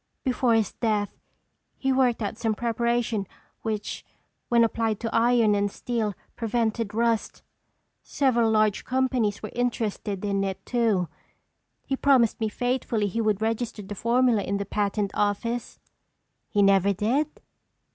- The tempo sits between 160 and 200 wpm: No, slow, 135 wpm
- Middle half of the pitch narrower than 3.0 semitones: Yes, narrow, 2.6 semitones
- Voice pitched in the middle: No, high, 225 Hz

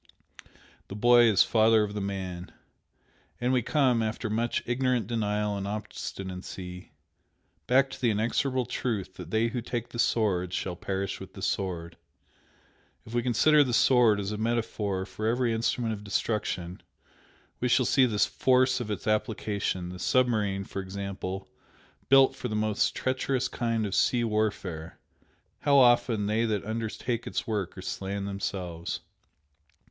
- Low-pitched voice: Yes, low, 110 Hz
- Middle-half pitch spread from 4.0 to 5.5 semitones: No, average, 3.6 semitones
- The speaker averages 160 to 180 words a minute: No, average, 150 wpm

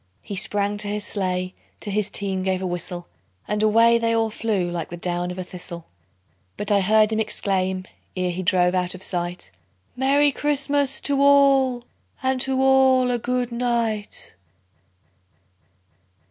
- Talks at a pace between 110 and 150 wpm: No, average, 160 wpm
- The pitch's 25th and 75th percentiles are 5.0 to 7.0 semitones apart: Yes, average, 5.3 semitones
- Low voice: No, high, 210 Hz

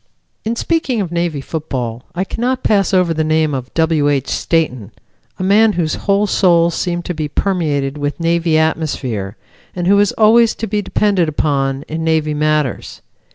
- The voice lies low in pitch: No, medium, 165 Hz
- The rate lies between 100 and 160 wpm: No, average, 170 wpm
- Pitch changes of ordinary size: Yes, average, 4.7 semitones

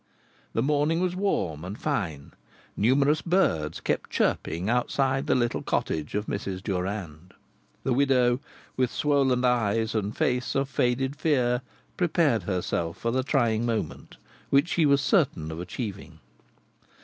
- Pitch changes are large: Yes, wide, 5.8 semitones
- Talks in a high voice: No, low, 120 Hz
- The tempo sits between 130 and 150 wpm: Yes, slow, 135 wpm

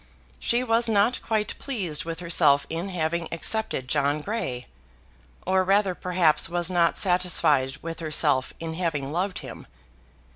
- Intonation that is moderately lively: Yes, average, 4.2 semitones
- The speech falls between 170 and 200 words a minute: No, average, 140 wpm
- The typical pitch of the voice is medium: Yes, medium, 170 Hz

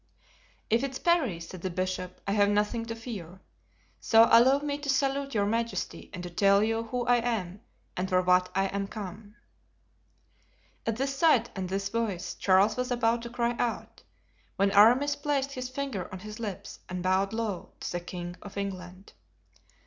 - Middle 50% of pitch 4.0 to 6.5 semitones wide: Yes, average, 4.4 semitones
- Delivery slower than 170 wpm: No, average, 180 wpm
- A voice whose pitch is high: Yes, high, 215 Hz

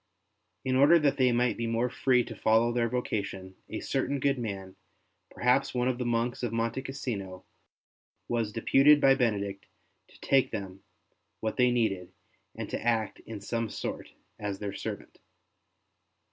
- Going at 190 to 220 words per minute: No, average, 160 wpm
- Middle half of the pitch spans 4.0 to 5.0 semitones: No, average, 3.4 semitones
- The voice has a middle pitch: No, low, 120 Hz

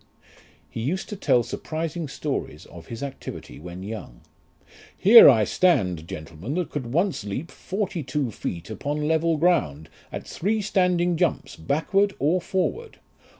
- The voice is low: No, medium, 150 Hz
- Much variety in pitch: Yes, wide, 8.8 semitones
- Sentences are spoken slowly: No, average, 145 wpm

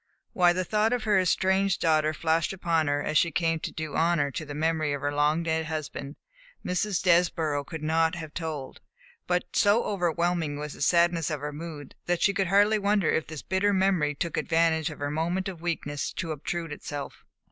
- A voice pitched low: No, medium, 165 Hz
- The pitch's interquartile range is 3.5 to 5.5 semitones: No, average, 2.9 semitones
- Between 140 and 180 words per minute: No, average, 200 wpm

